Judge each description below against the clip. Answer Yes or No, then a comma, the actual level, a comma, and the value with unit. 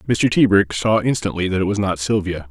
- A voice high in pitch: No, low, 100 Hz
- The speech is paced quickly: Yes, fast, 215 wpm